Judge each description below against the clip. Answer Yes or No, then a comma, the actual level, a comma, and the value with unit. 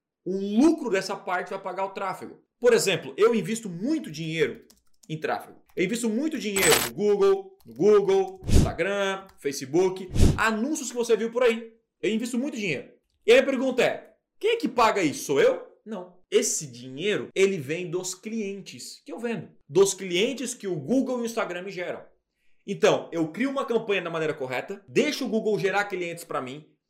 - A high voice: Yes, high, 210 Hz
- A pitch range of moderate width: No, wide, 6.0 semitones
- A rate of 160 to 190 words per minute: Yes, fast, 185 wpm